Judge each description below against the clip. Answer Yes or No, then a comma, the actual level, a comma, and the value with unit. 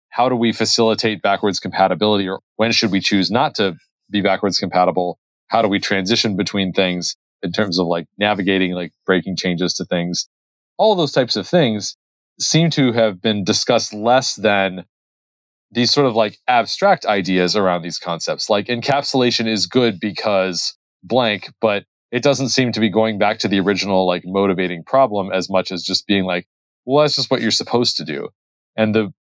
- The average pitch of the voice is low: Yes, low, 100 Hz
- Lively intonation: No, average, 3.5 semitones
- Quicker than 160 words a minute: Yes, average, 185 wpm